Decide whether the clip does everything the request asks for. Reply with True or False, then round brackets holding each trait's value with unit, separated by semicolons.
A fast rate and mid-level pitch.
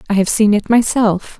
False (215 wpm; 210 Hz)